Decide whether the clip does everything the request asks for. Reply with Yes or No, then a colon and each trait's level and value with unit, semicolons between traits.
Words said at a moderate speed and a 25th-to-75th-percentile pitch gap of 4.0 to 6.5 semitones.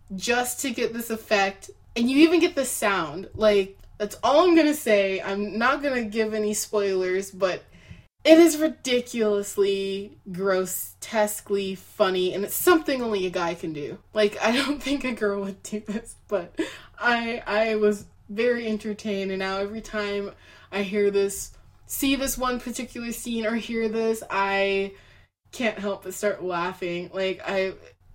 No: average, 160 wpm; average, 3.5 semitones